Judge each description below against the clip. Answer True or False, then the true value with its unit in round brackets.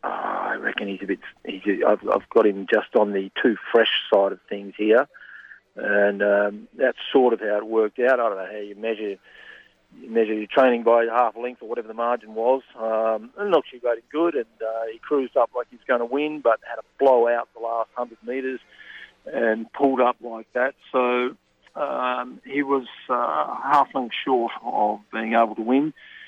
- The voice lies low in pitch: True (115 Hz)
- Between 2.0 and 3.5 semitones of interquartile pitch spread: True (2.7 semitones)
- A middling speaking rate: False (210 wpm)